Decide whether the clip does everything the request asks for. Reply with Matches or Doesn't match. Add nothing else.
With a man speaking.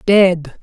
Matches